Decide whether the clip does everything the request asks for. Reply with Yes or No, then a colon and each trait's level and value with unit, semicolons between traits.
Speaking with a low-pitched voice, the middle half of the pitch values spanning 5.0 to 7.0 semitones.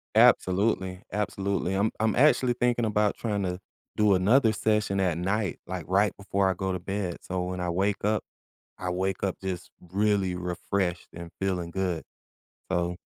No: very low, 95 Hz; narrow, 2.4 semitones